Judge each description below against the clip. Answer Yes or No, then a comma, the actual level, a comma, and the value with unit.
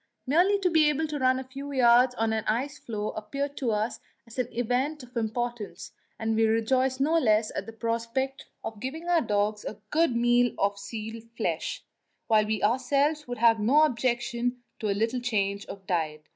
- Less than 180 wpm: No, average, 185 wpm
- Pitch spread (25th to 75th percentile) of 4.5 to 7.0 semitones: No, average, 3.6 semitones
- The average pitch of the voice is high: Yes, high, 240 Hz